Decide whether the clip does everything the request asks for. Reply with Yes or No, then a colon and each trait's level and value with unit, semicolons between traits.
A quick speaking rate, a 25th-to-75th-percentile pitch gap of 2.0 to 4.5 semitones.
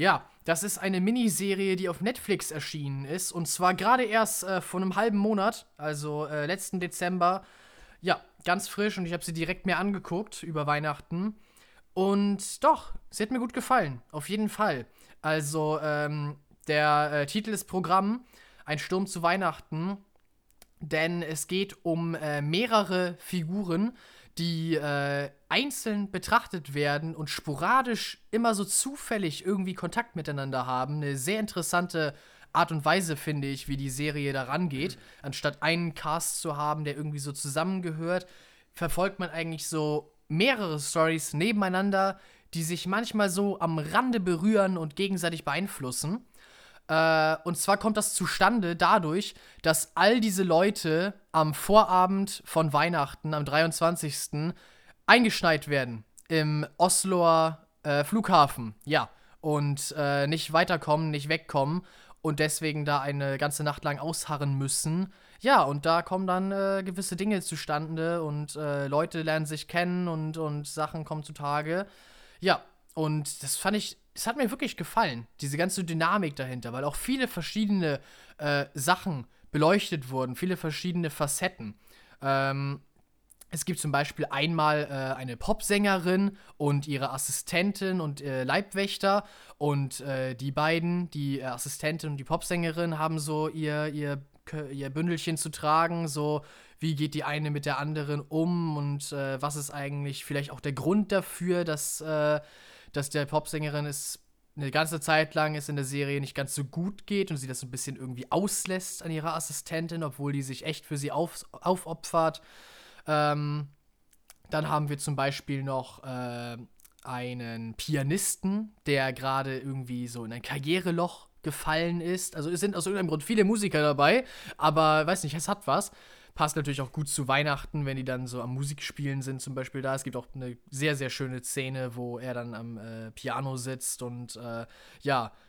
No: average, 155 wpm; average, 4.2 semitones